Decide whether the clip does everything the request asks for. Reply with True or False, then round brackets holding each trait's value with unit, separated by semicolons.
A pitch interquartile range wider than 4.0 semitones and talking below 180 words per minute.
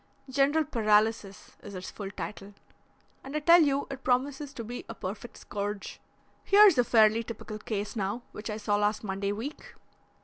True (4.7 semitones; 170 wpm)